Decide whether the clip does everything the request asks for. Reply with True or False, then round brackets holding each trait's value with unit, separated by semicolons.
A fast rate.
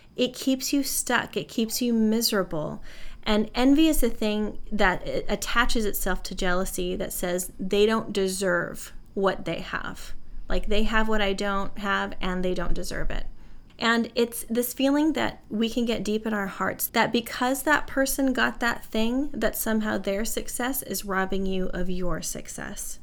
False (175 wpm)